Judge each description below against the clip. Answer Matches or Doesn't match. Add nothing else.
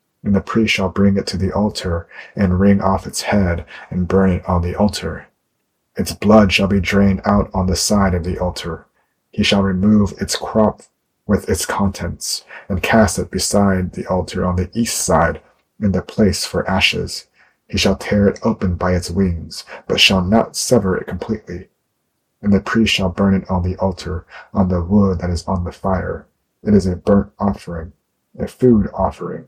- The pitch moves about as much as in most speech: Doesn't match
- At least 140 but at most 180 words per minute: Doesn't match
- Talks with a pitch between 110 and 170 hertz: Doesn't match